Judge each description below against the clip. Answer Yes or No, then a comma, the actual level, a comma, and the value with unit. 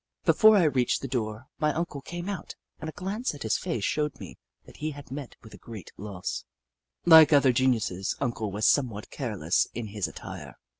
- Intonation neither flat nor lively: No, wide, 5.9 semitones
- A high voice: No, low, 130 Hz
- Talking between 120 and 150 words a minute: No, average, 195 wpm